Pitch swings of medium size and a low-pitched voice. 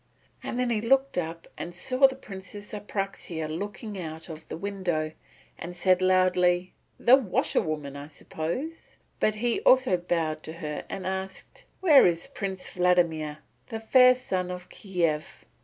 No: average, 4.3 semitones; medium, 185 Hz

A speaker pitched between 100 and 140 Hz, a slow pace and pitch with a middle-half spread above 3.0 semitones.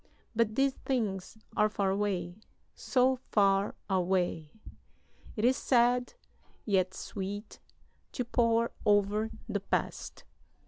No: high, 210 Hz; slow, 105 wpm; average, 3.6 semitones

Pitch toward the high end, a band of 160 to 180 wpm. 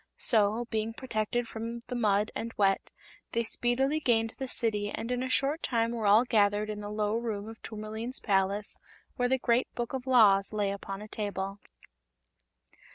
Yes: high, 225 Hz; average, 175 wpm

